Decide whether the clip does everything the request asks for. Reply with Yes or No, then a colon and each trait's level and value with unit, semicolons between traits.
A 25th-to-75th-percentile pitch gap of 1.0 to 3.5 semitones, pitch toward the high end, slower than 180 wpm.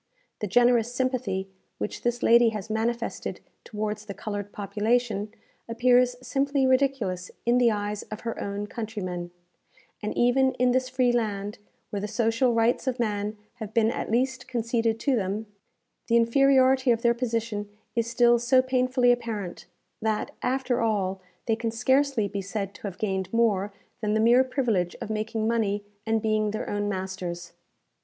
Yes: average, 3.0 semitones; high, 225 Hz; average, 160 wpm